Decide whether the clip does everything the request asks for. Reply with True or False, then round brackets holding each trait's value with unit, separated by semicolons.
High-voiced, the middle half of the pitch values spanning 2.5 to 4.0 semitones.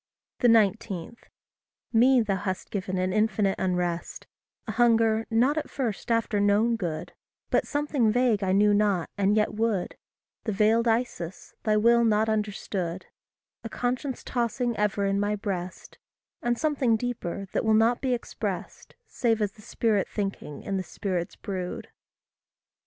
True (215 Hz; 3.0 semitones)